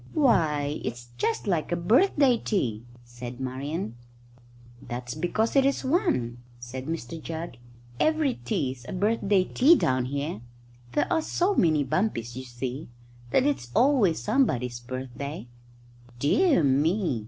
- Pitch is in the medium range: Yes, medium, 155 Hz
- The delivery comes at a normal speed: No, slow, 130 wpm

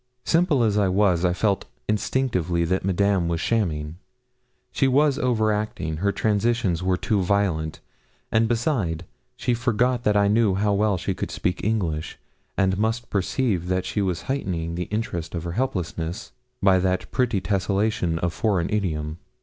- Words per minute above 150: Yes, average, 160 wpm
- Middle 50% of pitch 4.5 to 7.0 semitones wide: No, average, 4.0 semitones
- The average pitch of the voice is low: Yes, low, 100 Hz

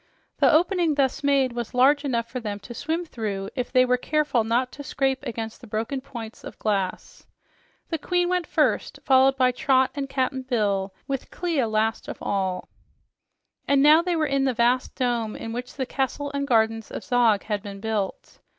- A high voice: Yes, very high, 255 Hz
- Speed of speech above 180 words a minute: Yes, average, 190 wpm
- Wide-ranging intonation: No, average, 4.0 semitones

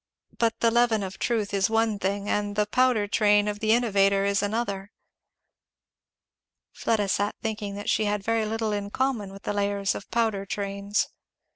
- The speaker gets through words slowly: No, average, 170 wpm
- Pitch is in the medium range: No, high, 205 Hz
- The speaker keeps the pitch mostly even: Yes, narrow, 1.8 semitones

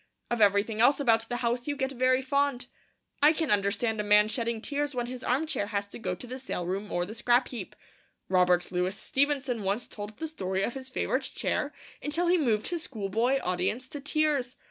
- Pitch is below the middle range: No, high, 240 Hz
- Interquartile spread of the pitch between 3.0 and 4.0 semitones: No, average, 4.8 semitones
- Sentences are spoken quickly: Yes, fast, 210 wpm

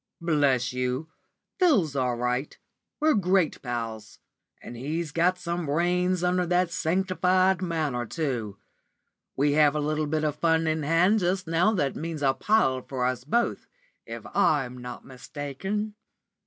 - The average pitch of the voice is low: No, medium, 155 Hz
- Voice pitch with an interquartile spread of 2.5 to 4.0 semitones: No, average, 5.3 semitones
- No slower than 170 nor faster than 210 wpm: No, average, 145 wpm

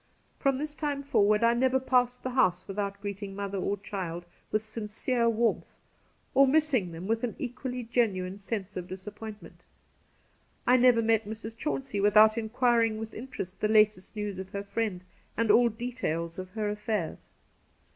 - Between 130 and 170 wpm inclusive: Yes, average, 165 wpm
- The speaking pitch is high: Yes, high, 220 Hz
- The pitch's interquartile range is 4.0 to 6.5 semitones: No, average, 3.5 semitones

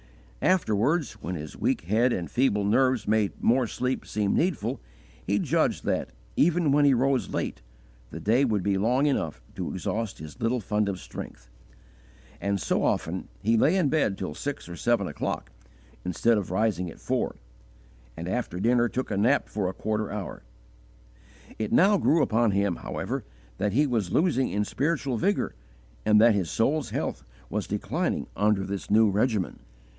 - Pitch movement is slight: No, average, 4.8 semitones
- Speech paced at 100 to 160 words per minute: No, average, 170 wpm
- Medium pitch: No, low, 110 Hz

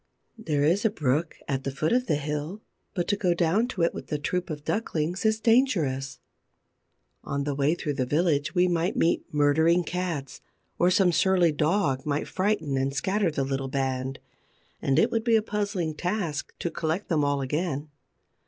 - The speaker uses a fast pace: No, average, 185 wpm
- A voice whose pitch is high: No, medium, 160 Hz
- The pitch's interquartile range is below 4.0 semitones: No, average, 4.6 semitones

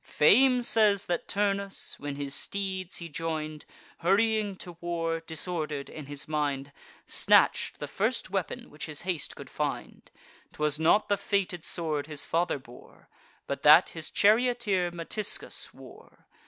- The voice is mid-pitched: Yes, medium, 170 Hz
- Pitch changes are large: No, average, 4.7 semitones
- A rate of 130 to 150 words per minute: Yes, average, 140 wpm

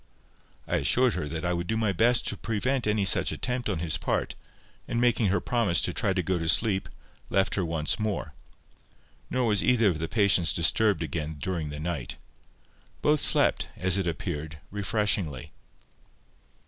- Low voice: Yes, very low, 95 Hz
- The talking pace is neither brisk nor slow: Yes, average, 170 wpm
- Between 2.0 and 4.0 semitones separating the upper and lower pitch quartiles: No, wide, 5.4 semitones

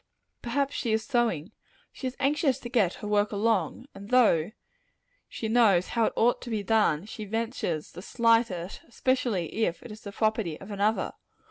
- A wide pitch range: No, average, 3.2 semitones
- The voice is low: No, high, 220 Hz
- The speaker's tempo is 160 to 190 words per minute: Yes, average, 180 wpm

